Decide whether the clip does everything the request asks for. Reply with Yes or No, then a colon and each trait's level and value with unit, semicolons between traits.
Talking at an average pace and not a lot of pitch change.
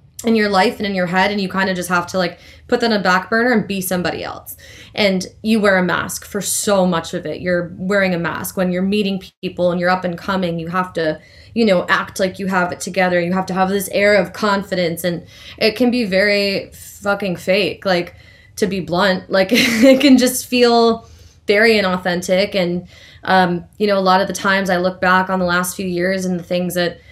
No: fast, 235 wpm; narrow, 2.1 semitones